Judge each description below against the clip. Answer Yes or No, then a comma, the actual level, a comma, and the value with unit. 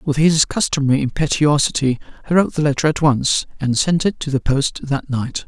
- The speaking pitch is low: No, medium, 145 Hz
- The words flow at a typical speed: Yes, average, 195 wpm